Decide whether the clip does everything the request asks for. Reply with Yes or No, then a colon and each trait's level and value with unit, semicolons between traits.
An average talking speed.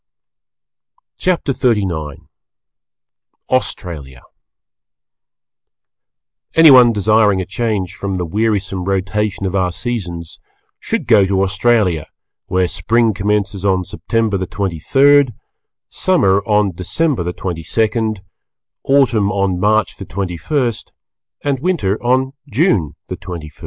No: slow, 115 wpm